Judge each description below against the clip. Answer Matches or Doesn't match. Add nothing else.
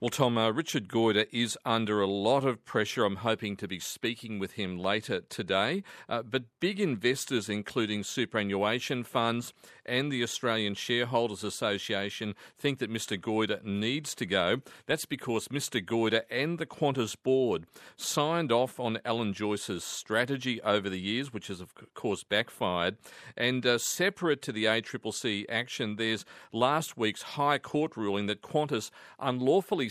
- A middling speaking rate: Matches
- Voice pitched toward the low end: Matches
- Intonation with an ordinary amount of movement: Matches